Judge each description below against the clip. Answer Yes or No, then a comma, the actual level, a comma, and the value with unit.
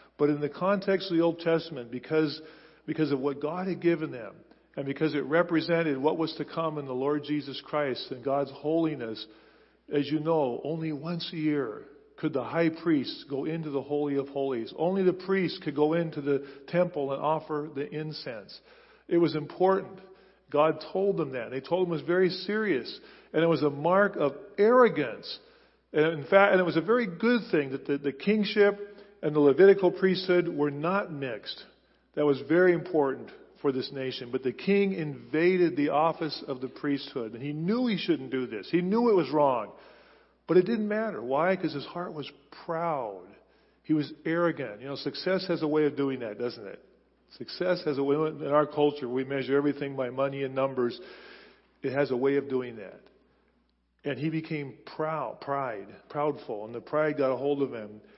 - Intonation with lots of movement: No, average, 4.0 semitones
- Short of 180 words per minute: No, average, 195 wpm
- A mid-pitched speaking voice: Yes, medium, 155 Hz